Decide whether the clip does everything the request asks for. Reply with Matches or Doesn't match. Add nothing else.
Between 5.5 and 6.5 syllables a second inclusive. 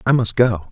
Doesn't match